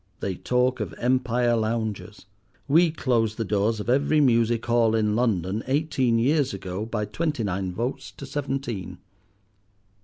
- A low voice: Yes, low, 115 Hz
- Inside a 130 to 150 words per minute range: Yes, average, 145 wpm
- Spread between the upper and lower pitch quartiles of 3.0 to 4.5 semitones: Yes, average, 3.4 semitones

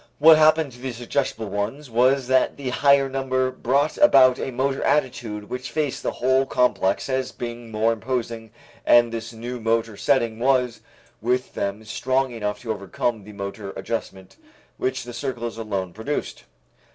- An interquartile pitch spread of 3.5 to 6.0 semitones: No, average, 2.8 semitones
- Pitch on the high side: No, low, 125 Hz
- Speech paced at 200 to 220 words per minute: No, average, 160 wpm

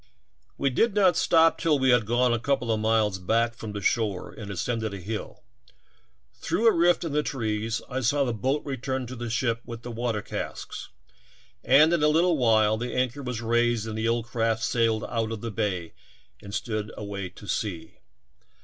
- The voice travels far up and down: No, average, 3.2 semitones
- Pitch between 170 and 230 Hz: No, low, 115 Hz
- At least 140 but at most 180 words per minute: No, average, 195 wpm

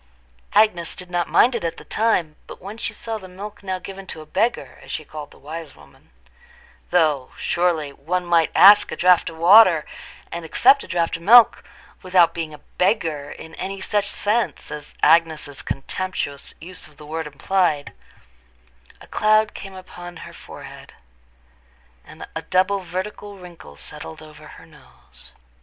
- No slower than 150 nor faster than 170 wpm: Yes, average, 160 wpm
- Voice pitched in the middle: Yes, medium, 170 Hz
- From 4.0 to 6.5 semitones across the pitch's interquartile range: Yes, average, 4.3 semitones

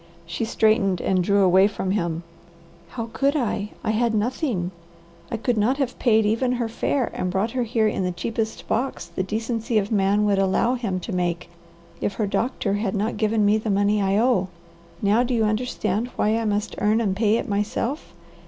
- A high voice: Yes, high, 215 Hz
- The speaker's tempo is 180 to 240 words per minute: Yes, average, 200 wpm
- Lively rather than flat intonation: No, average, 2.8 semitones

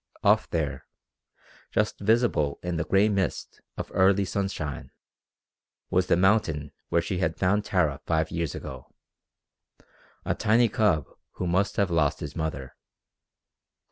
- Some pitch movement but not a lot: Yes, average, 4.2 semitones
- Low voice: Yes, very low, 90 Hz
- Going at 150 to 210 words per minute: No, slow, 135 wpm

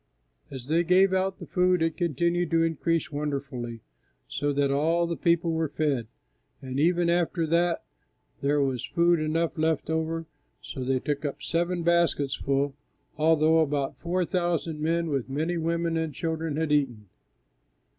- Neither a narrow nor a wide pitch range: Yes, average, 3.0 semitones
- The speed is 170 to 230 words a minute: No, average, 155 wpm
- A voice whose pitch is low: No, medium, 160 Hz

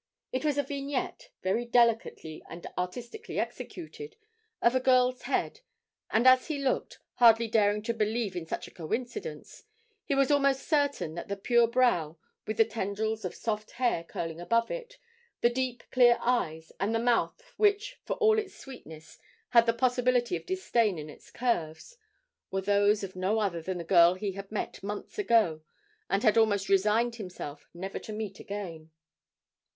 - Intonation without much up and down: No, average, 4.9 semitones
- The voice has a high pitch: Yes, high, 225 Hz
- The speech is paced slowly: No, average, 170 wpm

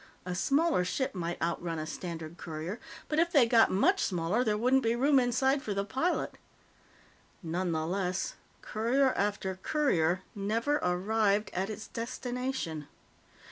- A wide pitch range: Yes, wide, 6.3 semitones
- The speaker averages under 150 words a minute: Yes, average, 140 wpm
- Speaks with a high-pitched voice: Yes, high, 210 Hz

